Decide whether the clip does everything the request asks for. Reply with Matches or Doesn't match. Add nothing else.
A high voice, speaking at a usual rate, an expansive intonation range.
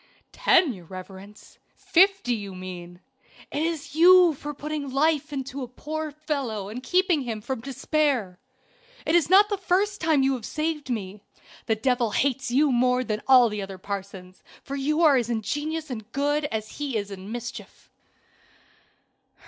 Matches